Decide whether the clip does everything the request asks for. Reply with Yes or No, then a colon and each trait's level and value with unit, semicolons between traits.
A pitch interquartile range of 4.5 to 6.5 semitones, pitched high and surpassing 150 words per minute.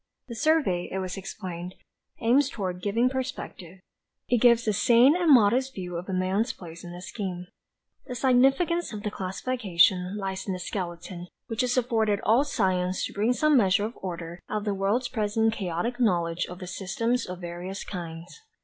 Yes: average, 5.1 semitones; high, 205 Hz; average, 175 wpm